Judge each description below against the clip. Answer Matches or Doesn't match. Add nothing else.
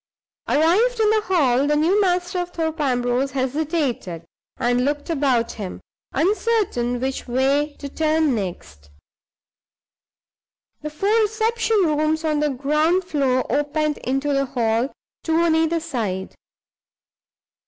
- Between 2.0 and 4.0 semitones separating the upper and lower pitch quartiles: Doesn't match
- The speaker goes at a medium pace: Doesn't match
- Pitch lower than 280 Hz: Doesn't match